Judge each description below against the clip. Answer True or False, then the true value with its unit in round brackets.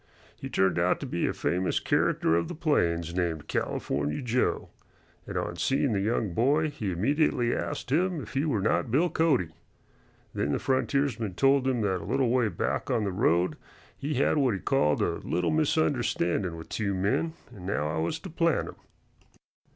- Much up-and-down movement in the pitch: True (7.6 semitones)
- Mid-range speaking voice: False (115 Hz)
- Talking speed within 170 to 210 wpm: True (185 wpm)